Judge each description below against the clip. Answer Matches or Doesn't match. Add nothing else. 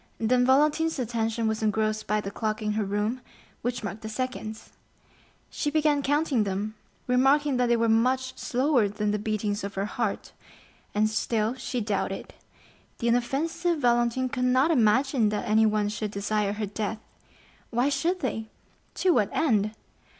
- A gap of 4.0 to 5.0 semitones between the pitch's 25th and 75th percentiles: Doesn't match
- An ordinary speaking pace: Matches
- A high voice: Matches